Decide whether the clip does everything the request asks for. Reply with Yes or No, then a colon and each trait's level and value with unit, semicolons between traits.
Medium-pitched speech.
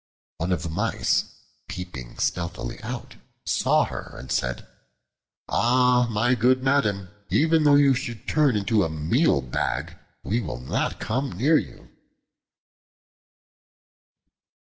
No: low, 115 Hz